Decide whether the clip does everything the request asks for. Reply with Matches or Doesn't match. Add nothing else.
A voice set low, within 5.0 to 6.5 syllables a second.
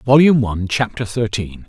Matches